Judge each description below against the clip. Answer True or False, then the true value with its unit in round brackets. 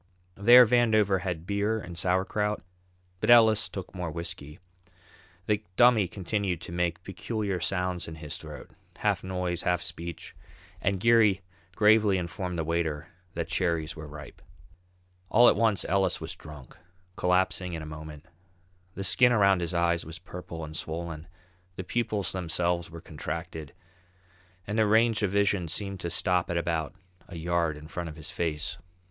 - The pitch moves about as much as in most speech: True (3.5 semitones)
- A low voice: True (90 Hz)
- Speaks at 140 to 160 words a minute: True (155 wpm)